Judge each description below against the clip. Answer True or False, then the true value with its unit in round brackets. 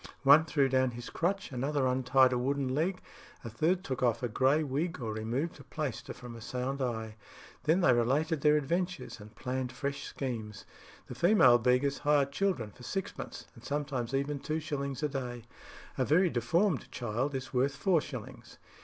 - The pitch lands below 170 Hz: True (135 Hz)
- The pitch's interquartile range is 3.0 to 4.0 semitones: True (3.5 semitones)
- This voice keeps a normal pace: True (180 wpm)